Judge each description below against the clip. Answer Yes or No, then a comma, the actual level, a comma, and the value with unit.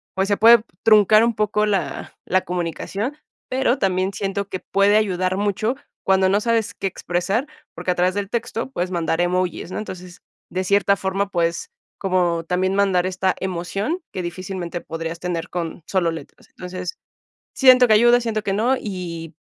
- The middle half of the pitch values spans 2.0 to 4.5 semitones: Yes, average, 2.9 semitones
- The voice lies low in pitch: No, high, 190 Hz